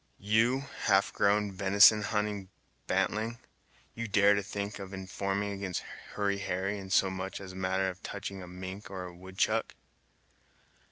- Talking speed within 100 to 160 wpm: Yes, average, 150 wpm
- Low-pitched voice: Yes, low, 100 Hz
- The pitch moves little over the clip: Yes, narrow, 1.5 semitones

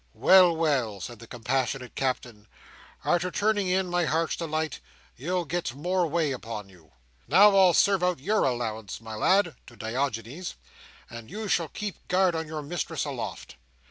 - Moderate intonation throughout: No, wide, 7.1 semitones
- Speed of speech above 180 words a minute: No, average, 160 wpm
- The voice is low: No, medium, 155 Hz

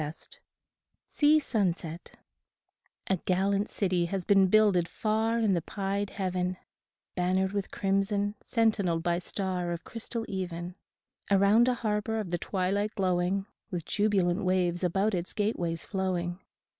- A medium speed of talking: No, slow, 130 wpm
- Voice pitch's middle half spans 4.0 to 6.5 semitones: No, average, 2.7 semitones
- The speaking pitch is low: No, high, 190 Hz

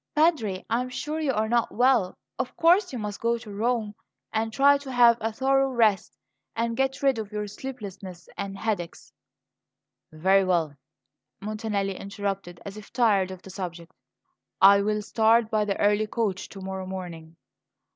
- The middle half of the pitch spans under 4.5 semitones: Yes, average, 3.6 semitones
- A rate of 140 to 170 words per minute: Yes, average, 165 wpm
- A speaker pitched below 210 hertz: No, high, 215 Hz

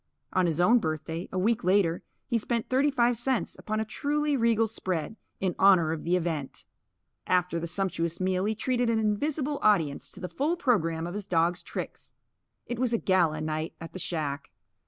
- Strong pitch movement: Yes, wide, 5.8 semitones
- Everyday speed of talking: Yes, average, 190 wpm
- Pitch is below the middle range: No, high, 190 Hz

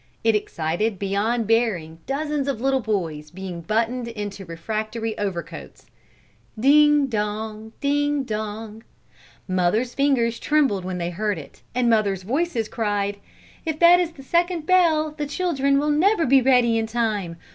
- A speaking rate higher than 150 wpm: No, average, 145 wpm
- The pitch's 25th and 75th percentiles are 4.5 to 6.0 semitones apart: Yes, wide, 5.5 semitones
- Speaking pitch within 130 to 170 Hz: No, high, 225 Hz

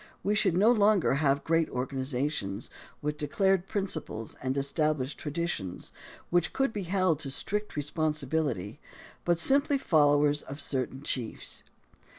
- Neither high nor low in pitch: Yes, medium, 150 Hz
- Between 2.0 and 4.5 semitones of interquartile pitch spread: No, average, 5.1 semitones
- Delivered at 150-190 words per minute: No, slow, 135 wpm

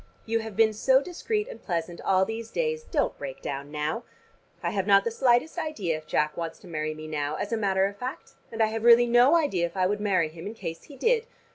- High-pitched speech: Yes, high, 205 Hz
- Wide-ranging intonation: Yes, wide, 6.3 semitones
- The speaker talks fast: Yes, fast, 245 wpm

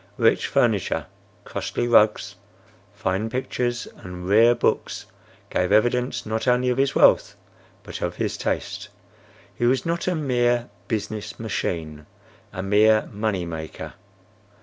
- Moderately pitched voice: No, low, 110 Hz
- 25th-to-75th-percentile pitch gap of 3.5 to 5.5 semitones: Yes, average, 3.8 semitones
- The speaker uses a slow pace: Yes, slow, 125 wpm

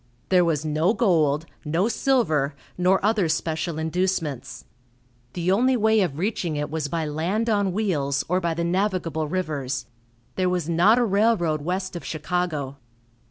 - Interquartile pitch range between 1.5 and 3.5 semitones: No, average, 3.9 semitones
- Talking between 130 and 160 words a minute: Yes, average, 155 wpm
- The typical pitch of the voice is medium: Yes, medium, 170 Hz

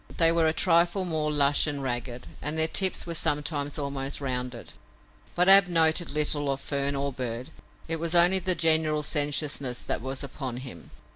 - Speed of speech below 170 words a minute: No, average, 180 wpm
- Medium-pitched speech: Yes, medium, 150 Hz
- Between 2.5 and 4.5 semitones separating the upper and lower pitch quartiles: Yes, average, 3.3 semitones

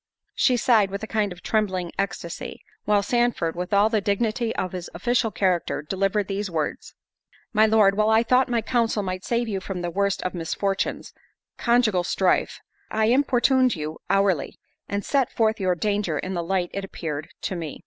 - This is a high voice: Yes, high, 200 Hz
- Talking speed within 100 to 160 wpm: No, average, 180 wpm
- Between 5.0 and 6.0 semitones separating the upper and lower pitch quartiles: No, average, 3.3 semitones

